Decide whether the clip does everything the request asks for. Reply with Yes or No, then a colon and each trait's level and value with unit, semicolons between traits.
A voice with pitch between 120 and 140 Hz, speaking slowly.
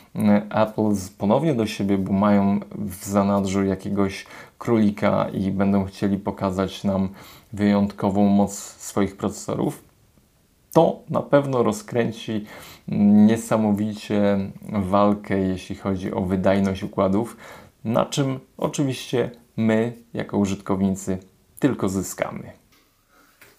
No: low, 100 Hz; slow, 95 wpm